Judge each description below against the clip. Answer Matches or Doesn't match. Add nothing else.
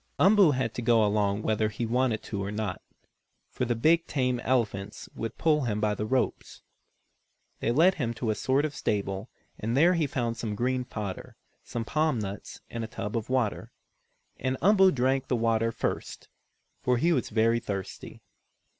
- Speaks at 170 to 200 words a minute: Matches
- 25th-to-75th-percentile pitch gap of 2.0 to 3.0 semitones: Doesn't match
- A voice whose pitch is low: Matches